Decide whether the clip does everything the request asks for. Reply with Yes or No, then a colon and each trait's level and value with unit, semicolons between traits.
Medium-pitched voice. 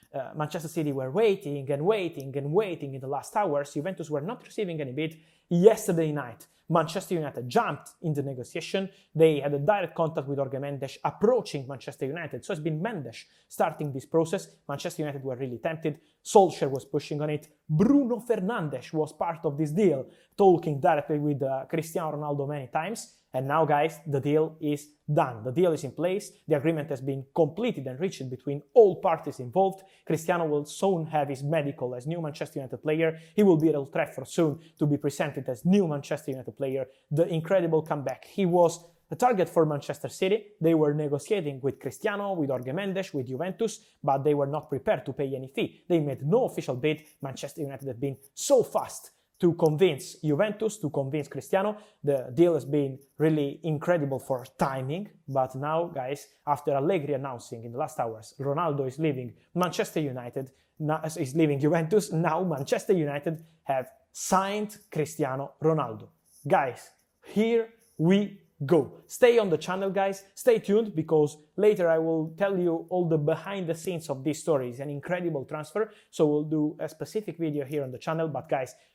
Yes: medium, 155 Hz